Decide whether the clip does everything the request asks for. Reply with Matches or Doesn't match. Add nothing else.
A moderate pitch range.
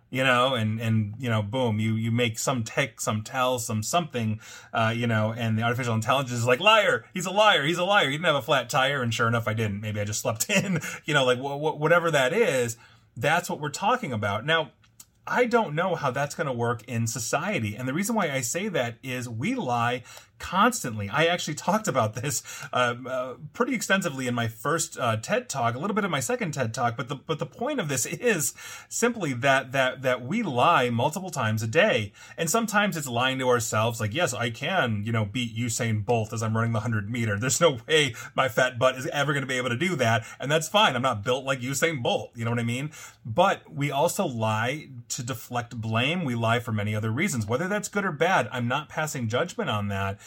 Doesn't match